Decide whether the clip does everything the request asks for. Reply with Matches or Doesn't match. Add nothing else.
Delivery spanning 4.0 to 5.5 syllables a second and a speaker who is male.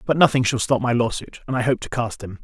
Doesn't match